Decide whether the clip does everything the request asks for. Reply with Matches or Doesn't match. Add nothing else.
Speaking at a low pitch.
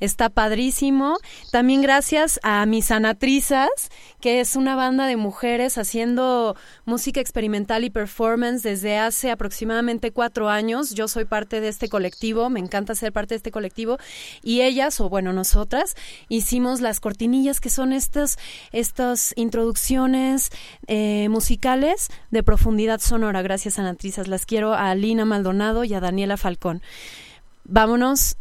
Doesn't match